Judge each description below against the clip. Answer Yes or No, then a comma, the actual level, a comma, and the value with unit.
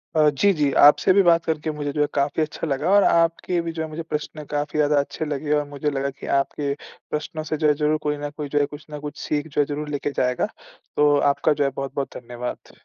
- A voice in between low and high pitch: Yes, medium, 150 Hz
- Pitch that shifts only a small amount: Yes, narrow, 1.4 semitones